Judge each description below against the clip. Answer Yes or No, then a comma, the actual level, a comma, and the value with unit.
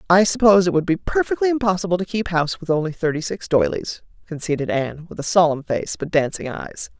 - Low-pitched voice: No, medium, 175 Hz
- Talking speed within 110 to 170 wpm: No, fast, 205 wpm